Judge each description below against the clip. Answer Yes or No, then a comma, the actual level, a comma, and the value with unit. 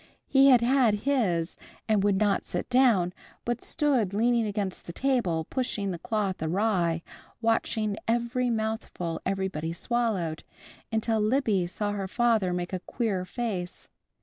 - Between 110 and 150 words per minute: Yes, average, 140 wpm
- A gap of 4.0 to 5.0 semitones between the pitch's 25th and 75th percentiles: Yes, average, 4.5 semitones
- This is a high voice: Yes, high, 210 Hz